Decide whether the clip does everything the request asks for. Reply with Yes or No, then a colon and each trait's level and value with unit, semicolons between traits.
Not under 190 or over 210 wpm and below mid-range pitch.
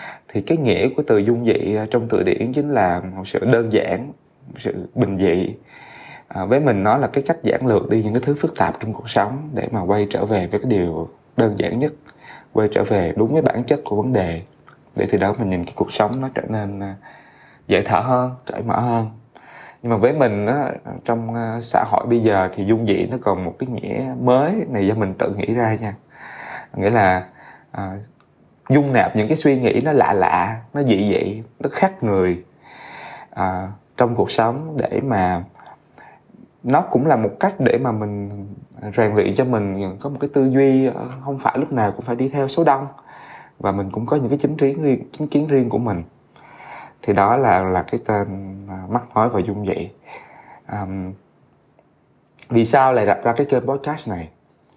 Yes: average, 205 wpm; low, 115 Hz